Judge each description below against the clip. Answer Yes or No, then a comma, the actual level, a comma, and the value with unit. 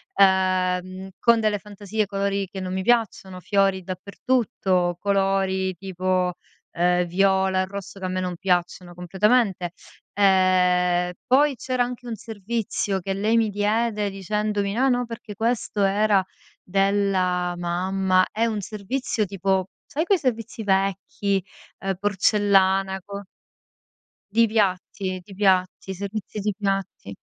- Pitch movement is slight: Yes, narrow, 2.2 semitones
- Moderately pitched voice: No, high, 195 Hz